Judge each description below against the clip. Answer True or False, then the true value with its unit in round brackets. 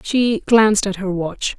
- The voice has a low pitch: False (205 Hz)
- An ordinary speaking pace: True (190 wpm)